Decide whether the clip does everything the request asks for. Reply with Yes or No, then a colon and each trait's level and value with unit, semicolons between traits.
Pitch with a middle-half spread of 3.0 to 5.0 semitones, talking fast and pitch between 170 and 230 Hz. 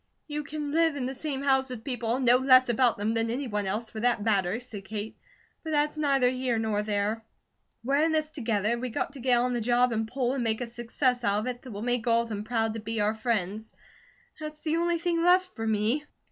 No: average, 3.7 semitones; fast, 245 wpm; high, 245 Hz